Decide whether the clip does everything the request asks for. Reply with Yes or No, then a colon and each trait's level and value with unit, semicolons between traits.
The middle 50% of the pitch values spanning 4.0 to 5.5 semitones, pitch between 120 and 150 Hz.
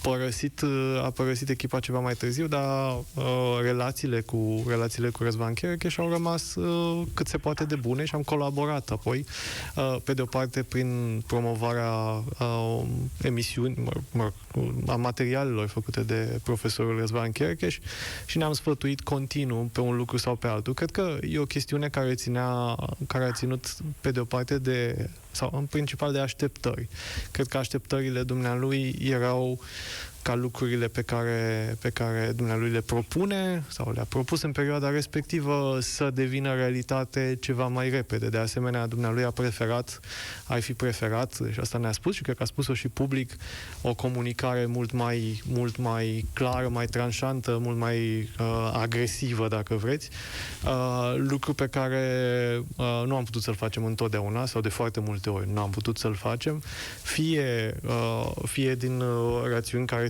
No: narrow, 2.5 semitones; low, 125 Hz